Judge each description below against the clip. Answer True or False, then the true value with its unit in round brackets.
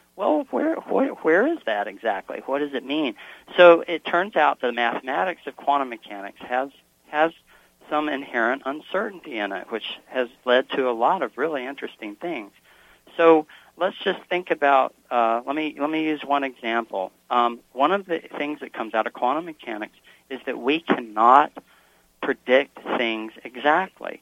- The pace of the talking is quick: False (170 wpm)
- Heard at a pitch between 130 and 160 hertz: True (140 Hz)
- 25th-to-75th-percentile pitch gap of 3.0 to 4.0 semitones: False (5.4 semitones)